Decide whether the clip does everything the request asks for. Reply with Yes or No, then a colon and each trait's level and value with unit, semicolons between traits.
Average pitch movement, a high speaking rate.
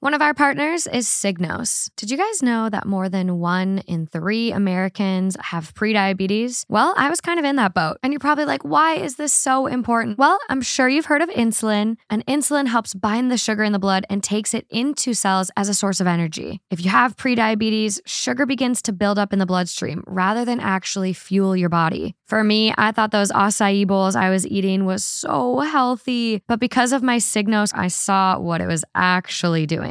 Yes: average, 4.6 semitones; fast, 210 wpm